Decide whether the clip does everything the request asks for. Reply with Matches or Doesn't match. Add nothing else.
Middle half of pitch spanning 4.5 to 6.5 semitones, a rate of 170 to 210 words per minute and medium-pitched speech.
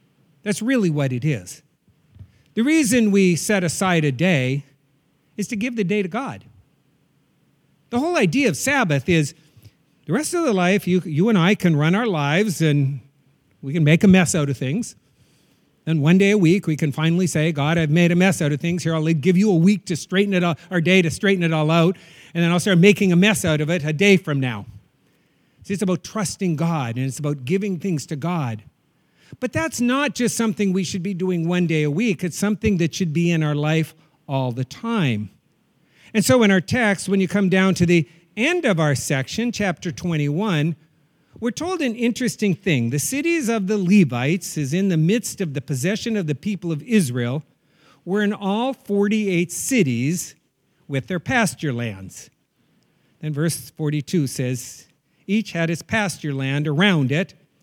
Matches